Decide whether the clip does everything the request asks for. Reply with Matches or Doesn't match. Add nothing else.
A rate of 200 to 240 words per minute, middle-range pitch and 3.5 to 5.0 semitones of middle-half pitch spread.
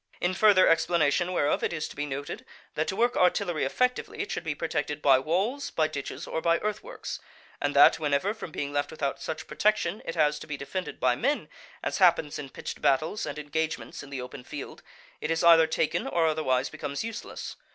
Matches